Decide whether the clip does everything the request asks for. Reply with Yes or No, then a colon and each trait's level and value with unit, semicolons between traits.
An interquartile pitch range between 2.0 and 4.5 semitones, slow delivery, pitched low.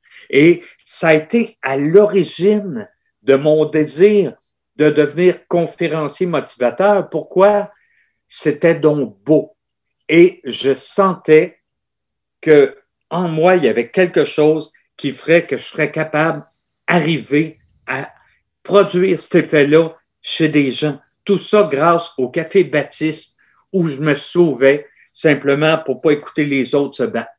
No: average, 4.2 semitones; slow, 130 wpm; medium, 160 Hz